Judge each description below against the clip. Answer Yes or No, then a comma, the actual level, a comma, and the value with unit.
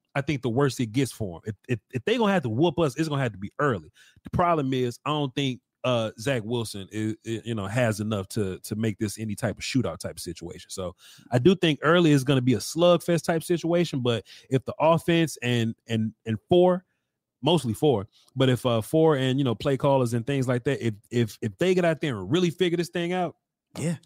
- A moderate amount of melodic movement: No, wide, 6.2 semitones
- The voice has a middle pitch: No, low, 130 Hz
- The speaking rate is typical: No, fast, 245 wpm